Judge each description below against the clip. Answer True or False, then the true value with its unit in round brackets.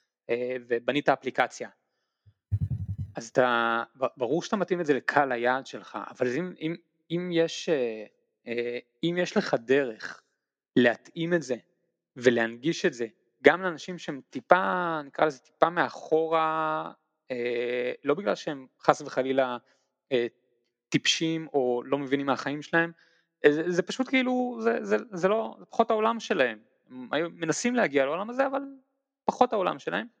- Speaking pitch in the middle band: True (150 Hz)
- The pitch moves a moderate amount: False (6.1 semitones)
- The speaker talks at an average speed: True (130 wpm)